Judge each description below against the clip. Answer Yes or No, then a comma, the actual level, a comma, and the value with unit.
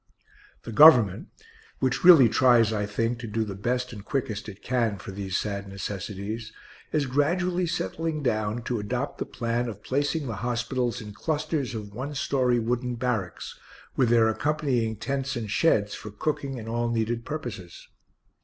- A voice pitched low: Yes, low, 120 Hz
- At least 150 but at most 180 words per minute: Yes, average, 165 wpm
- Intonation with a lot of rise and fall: No, average, 4.0 semitones